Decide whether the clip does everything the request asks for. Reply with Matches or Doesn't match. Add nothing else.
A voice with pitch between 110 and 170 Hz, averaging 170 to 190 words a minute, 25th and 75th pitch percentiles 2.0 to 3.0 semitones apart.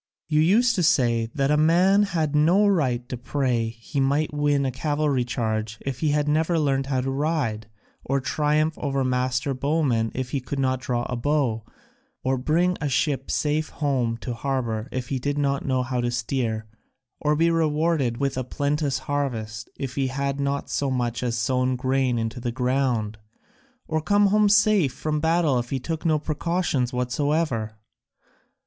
Doesn't match